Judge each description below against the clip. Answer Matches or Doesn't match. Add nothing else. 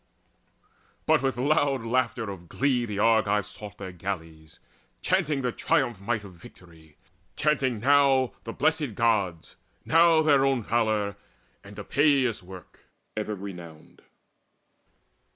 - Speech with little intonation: Doesn't match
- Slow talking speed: Matches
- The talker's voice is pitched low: Matches